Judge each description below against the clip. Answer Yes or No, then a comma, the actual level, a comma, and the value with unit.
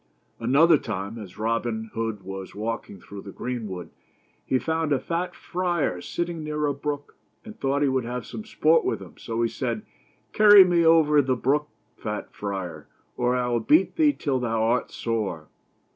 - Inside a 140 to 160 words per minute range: No, average, 180 wpm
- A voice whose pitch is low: Yes, low, 125 Hz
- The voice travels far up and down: Yes, wide, 5.9 semitones